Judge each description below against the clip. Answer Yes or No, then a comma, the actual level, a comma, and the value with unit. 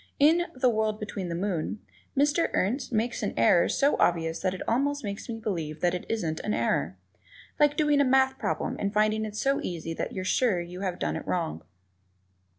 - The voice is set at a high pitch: Yes, high, 210 Hz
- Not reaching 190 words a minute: No, average, 200 wpm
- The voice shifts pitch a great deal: Yes, wide, 6.9 semitones